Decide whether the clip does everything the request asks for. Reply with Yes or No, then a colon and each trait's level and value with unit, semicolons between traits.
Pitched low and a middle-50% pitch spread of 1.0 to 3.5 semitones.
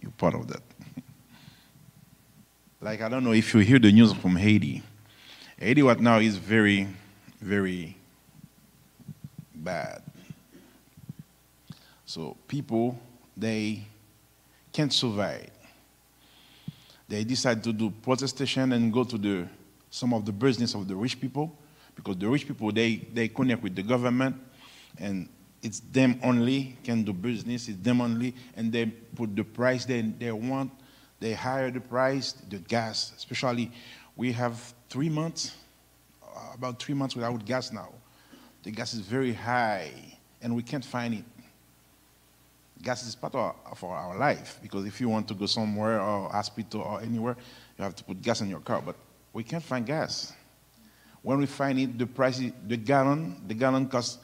Yes: low, 115 Hz; average, 3.2 semitones